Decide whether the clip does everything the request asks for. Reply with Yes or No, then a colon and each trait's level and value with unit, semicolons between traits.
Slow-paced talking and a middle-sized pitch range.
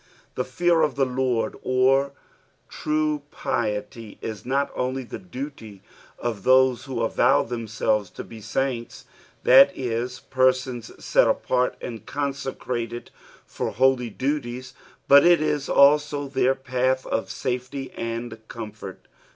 Yes: slow, 125 wpm; average, 3.0 semitones